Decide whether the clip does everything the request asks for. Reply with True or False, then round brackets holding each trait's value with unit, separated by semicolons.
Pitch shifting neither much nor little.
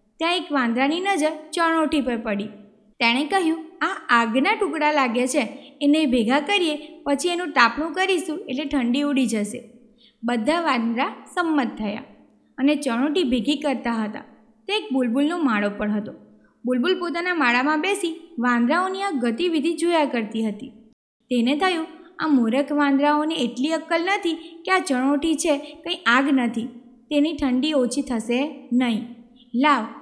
True (4.9 semitones)